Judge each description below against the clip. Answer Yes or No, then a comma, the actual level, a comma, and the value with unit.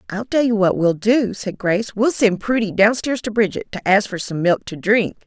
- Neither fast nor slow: No, fast, 250 wpm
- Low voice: No, high, 220 Hz